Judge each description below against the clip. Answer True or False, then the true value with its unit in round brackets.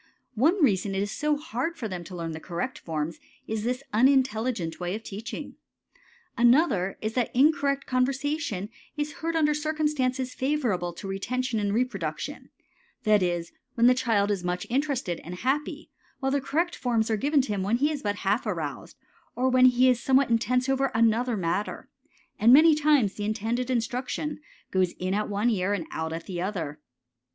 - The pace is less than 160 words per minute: False (180 wpm)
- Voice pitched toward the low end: False (235 Hz)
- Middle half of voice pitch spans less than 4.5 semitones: False (5.4 semitones)